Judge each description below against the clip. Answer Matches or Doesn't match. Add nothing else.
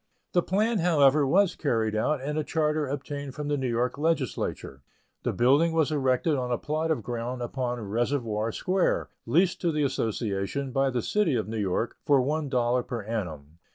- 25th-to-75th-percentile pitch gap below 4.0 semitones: Doesn't match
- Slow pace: Doesn't match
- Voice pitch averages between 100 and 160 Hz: Matches